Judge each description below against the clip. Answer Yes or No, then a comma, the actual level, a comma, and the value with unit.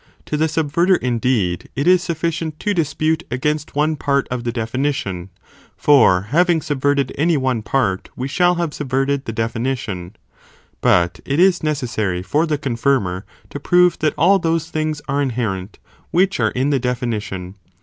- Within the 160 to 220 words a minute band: Yes, average, 165 wpm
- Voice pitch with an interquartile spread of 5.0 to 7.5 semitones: Yes, average, 5.3 semitones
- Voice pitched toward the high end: No, medium, 140 Hz